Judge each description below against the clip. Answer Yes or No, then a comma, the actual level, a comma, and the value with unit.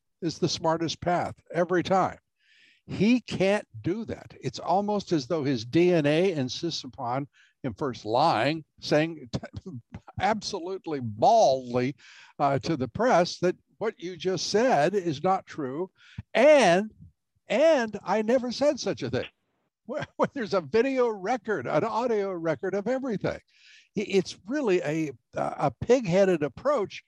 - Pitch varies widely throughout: Yes, wide, 5.8 semitones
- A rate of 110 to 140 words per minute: Yes, slow, 135 wpm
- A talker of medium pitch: Yes, medium, 175 Hz